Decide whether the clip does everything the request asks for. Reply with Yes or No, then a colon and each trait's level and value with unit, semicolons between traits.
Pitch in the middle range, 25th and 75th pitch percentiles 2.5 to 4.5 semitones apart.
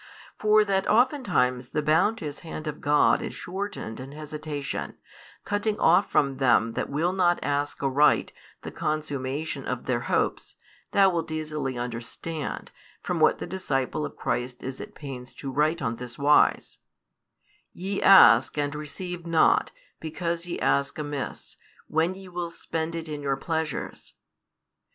Yes: medium, 150 Hz; average, 4.1 semitones